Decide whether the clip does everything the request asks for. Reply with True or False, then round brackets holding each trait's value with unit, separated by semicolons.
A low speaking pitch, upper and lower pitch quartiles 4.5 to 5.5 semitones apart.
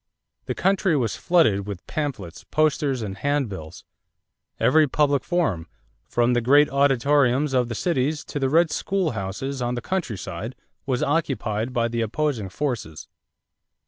True (130 Hz; 5.0 semitones)